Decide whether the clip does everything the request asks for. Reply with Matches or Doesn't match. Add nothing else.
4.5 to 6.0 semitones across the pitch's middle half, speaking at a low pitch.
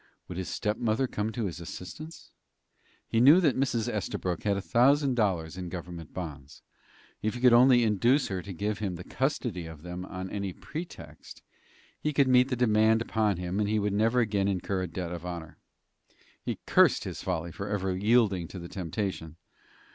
Matches